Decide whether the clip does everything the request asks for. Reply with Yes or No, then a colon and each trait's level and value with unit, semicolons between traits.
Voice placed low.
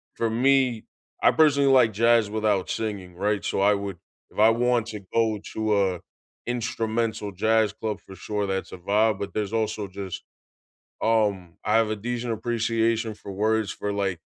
Yes: low, 110 Hz